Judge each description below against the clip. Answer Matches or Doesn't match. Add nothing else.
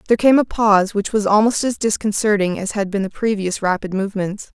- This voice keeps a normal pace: Doesn't match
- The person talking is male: Doesn't match